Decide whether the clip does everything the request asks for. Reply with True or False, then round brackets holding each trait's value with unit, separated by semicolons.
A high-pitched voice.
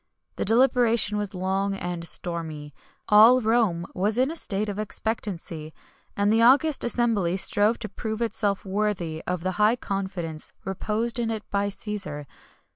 True (205 Hz)